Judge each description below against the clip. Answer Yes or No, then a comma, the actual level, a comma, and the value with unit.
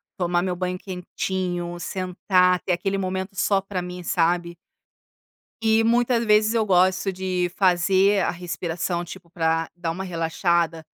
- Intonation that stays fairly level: Yes, narrow, 1.8 semitones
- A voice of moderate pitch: Yes, medium, 180 Hz